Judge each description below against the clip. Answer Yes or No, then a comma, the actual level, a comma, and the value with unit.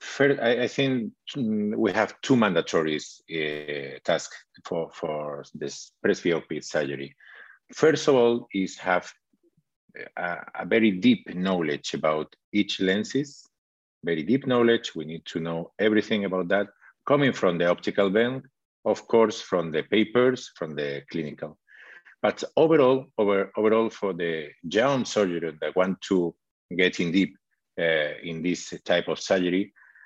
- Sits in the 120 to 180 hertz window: No, low, 100 Hz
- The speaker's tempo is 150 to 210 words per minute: No, average, 140 wpm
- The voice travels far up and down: Yes, wide, 6.1 semitones